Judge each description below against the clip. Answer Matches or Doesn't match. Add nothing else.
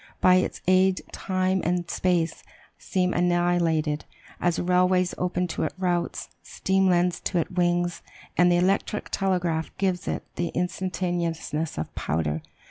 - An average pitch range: Doesn't match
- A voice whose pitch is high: Doesn't match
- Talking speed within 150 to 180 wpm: Doesn't match